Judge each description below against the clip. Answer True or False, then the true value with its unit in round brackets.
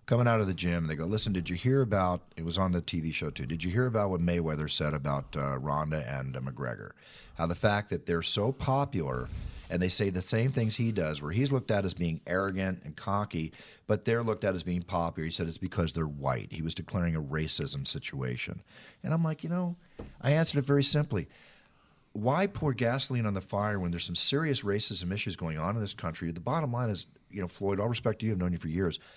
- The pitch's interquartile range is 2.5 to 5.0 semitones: False (5.5 semitones)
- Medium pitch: False (95 Hz)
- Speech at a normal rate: False (245 wpm)